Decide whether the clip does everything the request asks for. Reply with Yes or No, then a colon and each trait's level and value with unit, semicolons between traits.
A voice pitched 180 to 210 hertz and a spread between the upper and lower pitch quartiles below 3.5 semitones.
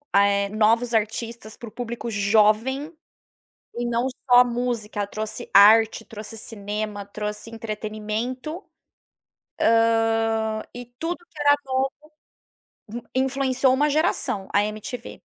No: high, 225 Hz; average, 3.1 semitones